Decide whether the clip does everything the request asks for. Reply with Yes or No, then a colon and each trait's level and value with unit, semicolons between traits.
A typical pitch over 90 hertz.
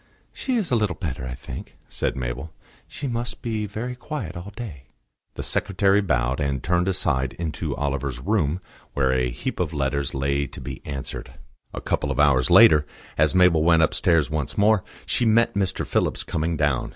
No: very low, 80 Hz